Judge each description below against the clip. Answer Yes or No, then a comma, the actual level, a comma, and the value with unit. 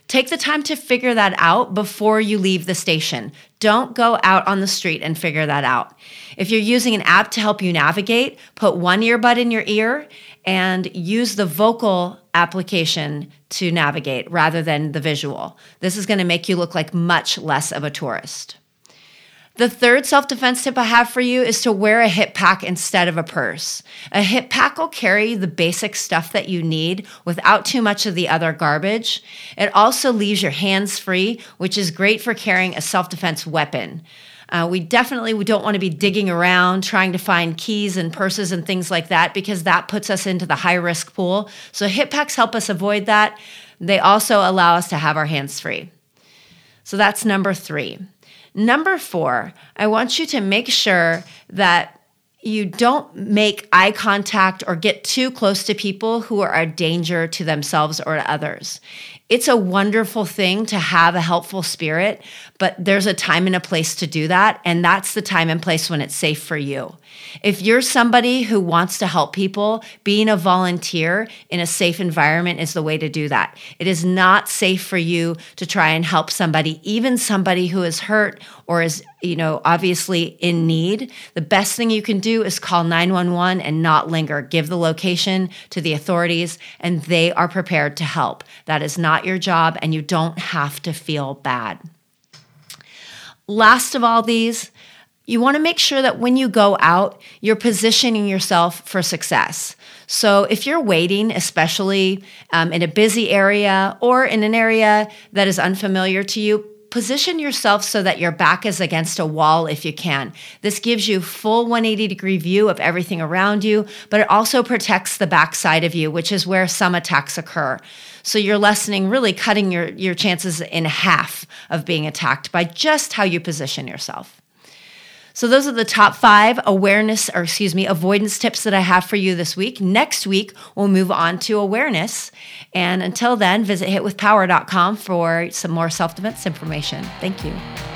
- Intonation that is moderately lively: Yes, average, 3.9 semitones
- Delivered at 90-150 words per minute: No, average, 190 wpm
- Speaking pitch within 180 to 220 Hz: Yes, high, 190 Hz